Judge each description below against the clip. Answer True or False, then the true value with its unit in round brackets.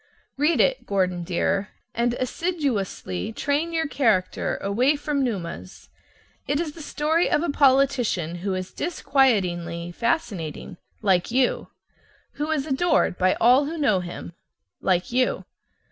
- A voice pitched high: True (245 Hz)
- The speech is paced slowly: True (130 wpm)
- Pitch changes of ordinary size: False (7.9 semitones)